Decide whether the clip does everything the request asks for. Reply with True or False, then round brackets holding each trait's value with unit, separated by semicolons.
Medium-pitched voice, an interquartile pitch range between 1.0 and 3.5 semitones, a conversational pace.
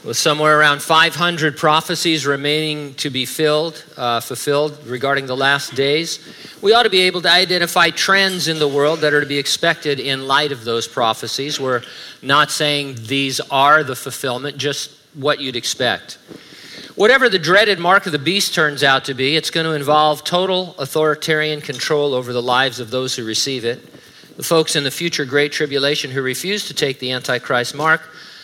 True (145 Hz; 2.8 semitones; 185 wpm)